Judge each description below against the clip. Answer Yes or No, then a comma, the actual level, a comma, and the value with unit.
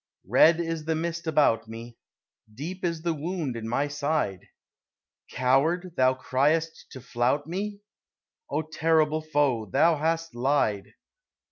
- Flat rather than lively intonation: No, average, 4.1 semitones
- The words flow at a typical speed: No, slow, 130 wpm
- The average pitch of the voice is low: No, medium, 150 Hz